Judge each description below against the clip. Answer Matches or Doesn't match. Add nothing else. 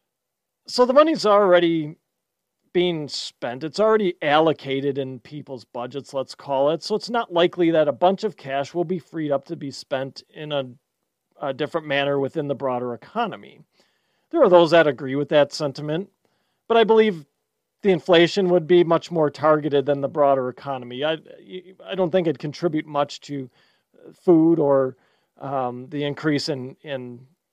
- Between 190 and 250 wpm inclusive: Doesn't match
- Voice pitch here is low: Doesn't match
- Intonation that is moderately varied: Matches